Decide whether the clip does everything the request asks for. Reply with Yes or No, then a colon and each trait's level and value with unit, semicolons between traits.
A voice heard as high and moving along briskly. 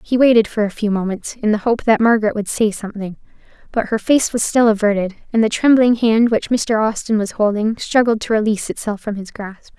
Yes: high, 220 Hz; fast, 220 wpm